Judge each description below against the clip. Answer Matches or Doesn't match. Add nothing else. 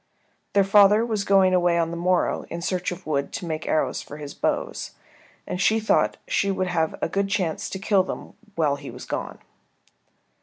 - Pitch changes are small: Doesn't match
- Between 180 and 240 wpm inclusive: Matches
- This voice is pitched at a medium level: Matches